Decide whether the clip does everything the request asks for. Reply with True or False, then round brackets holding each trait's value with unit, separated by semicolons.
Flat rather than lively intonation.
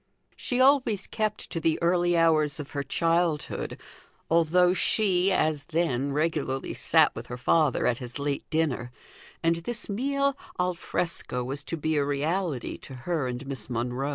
False (4.3 semitones)